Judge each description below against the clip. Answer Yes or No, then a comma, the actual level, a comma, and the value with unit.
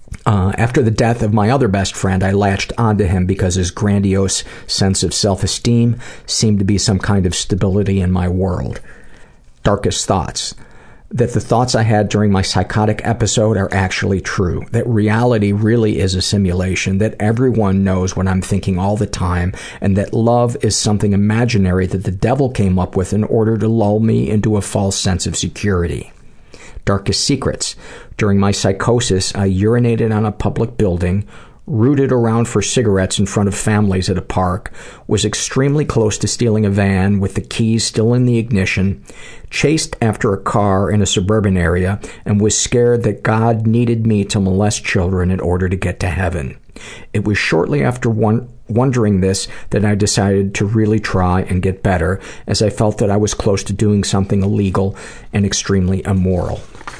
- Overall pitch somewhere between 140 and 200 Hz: No, low, 100 Hz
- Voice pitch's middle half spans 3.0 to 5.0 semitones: No, narrow, 2.5 semitones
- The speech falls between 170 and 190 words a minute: Yes, average, 180 wpm